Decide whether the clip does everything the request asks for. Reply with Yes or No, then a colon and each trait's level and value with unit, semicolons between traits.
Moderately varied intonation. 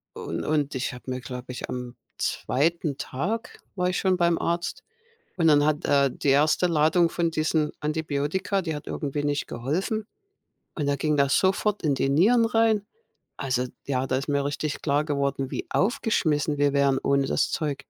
Yes: average, 3.5 semitones